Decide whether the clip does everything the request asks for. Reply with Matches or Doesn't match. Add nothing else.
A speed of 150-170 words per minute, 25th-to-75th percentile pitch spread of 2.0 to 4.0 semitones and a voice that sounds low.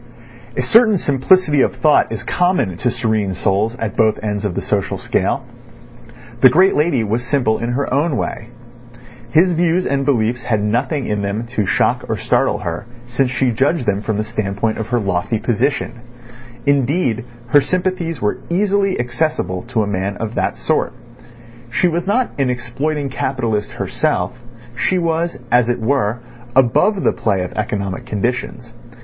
Doesn't match